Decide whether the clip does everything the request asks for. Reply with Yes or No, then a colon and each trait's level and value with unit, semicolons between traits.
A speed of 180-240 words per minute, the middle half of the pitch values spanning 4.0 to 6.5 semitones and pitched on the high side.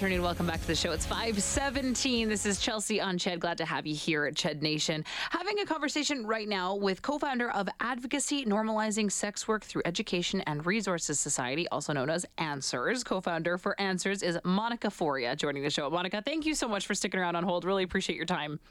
Yes: fast, 205 wpm; average, 4.6 semitones; high, 195 Hz